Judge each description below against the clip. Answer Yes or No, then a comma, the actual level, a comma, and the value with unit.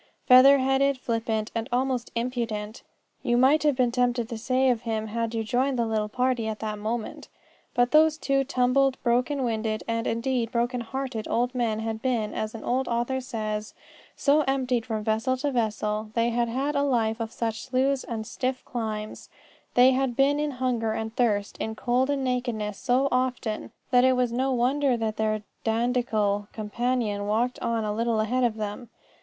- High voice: Yes, high, 240 Hz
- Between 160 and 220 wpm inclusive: Yes, average, 185 wpm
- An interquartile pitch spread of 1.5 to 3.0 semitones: Yes, average, 2.7 semitones